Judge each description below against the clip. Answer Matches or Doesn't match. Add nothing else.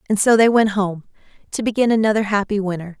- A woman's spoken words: Matches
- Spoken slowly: Doesn't match